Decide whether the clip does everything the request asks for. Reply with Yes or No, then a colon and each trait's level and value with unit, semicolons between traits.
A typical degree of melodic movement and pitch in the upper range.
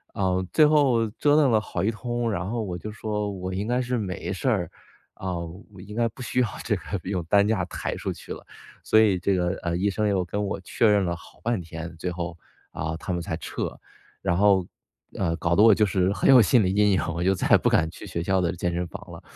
No: average, 3.8 semitones; low, 100 Hz